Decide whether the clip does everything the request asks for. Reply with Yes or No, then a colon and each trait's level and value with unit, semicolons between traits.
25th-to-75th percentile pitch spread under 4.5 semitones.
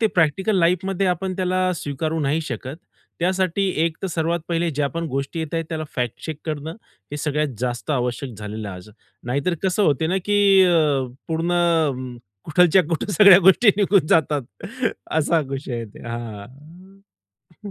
No: average, 4.8 semitones